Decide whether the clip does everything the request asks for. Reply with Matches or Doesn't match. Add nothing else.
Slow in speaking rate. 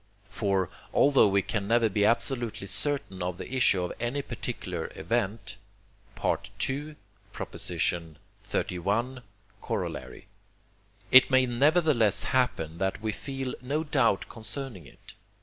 Matches